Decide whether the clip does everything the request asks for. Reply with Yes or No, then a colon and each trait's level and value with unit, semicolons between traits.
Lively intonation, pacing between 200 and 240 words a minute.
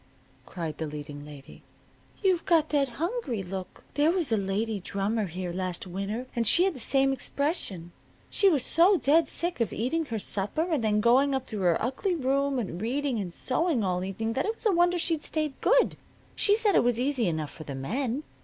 Yes: wide, 8.3 semitones; fast, 205 wpm